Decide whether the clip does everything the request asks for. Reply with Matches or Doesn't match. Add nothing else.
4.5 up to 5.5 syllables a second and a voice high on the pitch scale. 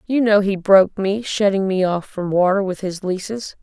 Matches